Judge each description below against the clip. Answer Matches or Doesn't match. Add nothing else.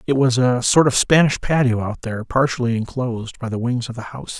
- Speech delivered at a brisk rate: Matches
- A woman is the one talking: Doesn't match